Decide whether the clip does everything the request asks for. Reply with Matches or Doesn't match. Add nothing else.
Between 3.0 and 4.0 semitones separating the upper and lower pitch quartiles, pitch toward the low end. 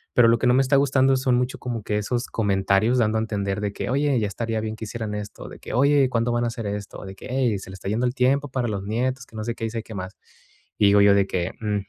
Matches